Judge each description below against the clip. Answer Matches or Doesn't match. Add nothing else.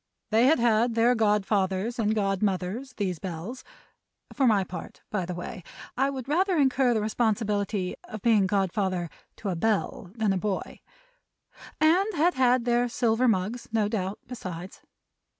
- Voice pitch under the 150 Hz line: Doesn't match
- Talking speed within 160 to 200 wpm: Doesn't match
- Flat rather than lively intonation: Doesn't match